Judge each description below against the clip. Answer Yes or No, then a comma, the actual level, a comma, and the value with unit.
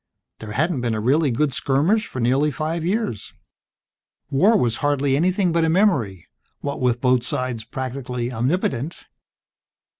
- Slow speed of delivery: No, average, 145 wpm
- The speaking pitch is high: No, low, 135 Hz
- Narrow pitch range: No, average, 5.1 semitones